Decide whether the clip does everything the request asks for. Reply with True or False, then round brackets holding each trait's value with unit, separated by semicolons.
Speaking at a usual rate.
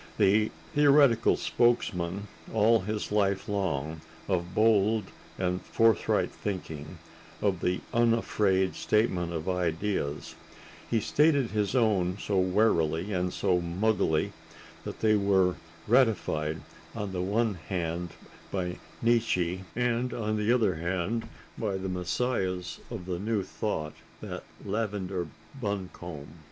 False (120 wpm)